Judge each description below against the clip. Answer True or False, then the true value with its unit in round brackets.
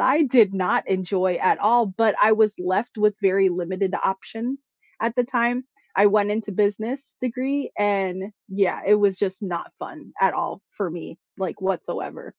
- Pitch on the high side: True (205 Hz)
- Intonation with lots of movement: False (3.3 semitones)